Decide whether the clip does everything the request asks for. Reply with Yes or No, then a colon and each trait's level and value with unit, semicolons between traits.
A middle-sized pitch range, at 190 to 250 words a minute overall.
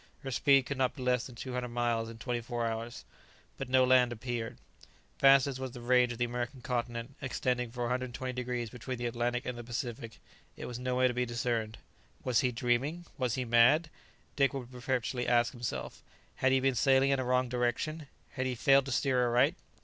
No: narrow, 1.5 semitones; fast, 205 wpm